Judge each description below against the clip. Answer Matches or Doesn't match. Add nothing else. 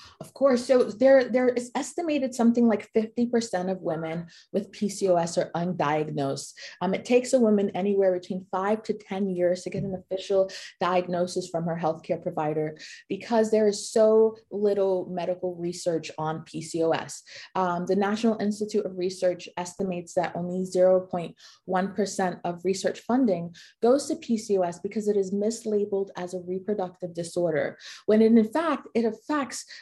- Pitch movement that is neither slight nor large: Matches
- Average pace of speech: Matches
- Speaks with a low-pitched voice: Doesn't match